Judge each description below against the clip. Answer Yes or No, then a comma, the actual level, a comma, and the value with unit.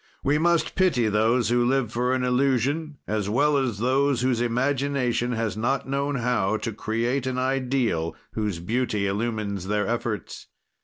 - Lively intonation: No, average, 3.6 semitones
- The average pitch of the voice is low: Yes, low, 120 Hz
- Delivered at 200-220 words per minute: No, average, 155 wpm